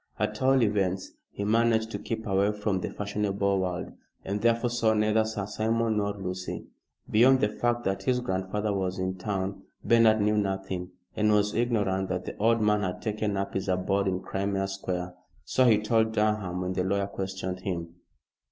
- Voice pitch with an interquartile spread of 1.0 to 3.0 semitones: Yes, narrow, 2.6 semitones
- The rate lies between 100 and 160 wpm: No, average, 180 wpm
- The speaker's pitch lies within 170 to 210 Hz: No, low, 100 Hz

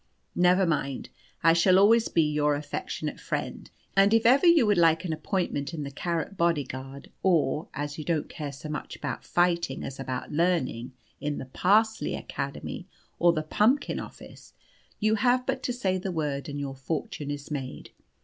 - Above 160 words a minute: Yes, average, 175 wpm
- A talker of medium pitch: Yes, medium, 165 Hz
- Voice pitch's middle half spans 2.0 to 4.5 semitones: No, average, 5.1 semitones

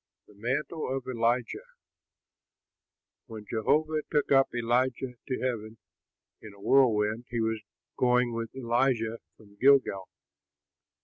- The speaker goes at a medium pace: No, slow, 115 wpm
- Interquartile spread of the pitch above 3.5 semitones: No, average, 2.9 semitones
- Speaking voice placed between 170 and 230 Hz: No, low, 120 Hz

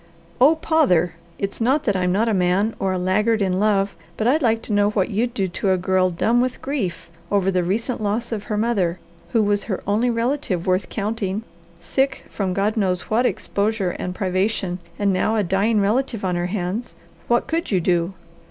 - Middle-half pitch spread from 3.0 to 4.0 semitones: Yes, average, 3.6 semitones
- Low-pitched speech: No, high, 205 Hz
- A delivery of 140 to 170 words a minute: No, average, 200 wpm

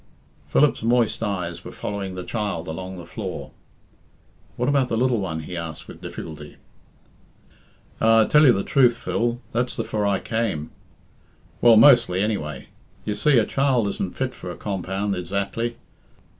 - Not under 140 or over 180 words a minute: Yes, average, 160 wpm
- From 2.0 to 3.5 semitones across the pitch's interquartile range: No, average, 4.7 semitones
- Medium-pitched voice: No, low, 105 Hz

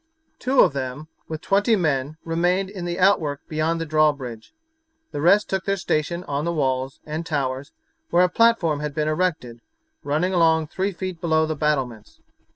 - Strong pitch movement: No, average, 3.8 semitones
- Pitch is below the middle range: No, medium, 160 Hz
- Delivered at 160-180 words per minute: Yes, average, 170 wpm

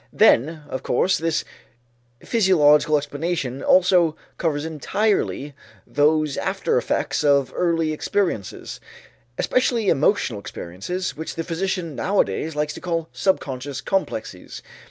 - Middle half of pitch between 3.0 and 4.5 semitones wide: Yes, average, 4.0 semitones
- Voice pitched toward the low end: No, medium, 155 Hz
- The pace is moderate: No, slow, 110 wpm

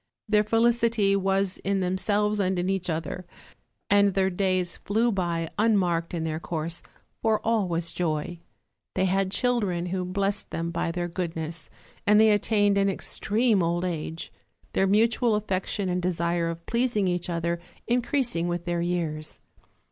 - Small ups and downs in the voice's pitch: No, average, 3.3 semitones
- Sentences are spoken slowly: No, average, 155 wpm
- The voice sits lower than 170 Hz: No, medium, 185 Hz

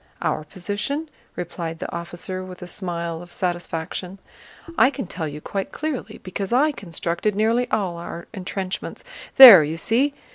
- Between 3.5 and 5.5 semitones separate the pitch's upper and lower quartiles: Yes, average, 4.4 semitones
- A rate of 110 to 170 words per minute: Yes, average, 150 wpm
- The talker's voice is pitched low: No, medium, 185 Hz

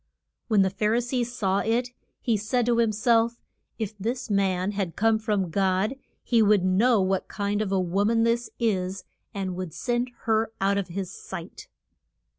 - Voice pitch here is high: Yes, high, 210 Hz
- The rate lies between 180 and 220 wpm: Yes, average, 185 wpm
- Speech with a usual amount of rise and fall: Yes, average, 3.3 semitones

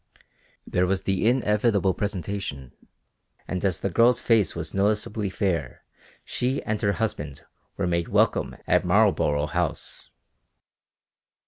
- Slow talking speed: Yes, slow, 120 wpm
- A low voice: Yes, low, 100 Hz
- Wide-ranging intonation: No, average, 3.3 semitones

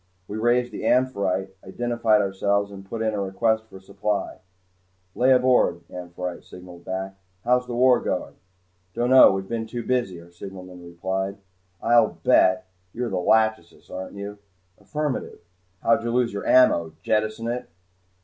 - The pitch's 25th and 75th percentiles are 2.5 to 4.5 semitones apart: Yes, average, 4.0 semitones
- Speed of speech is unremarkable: Yes, average, 150 wpm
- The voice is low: Yes, low, 105 Hz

